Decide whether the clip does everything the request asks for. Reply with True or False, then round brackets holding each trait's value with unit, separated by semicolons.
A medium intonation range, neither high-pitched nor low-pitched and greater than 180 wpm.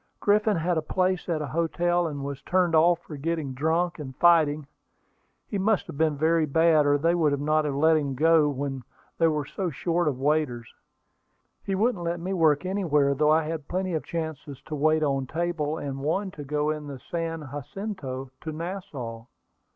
True (3.1 semitones; 155 Hz; 190 wpm)